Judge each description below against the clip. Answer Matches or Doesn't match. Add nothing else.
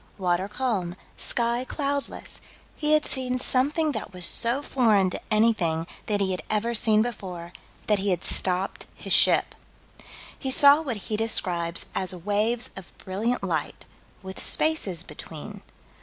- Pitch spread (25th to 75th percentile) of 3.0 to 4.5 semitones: Doesn't match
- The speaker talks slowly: Doesn't match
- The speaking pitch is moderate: Doesn't match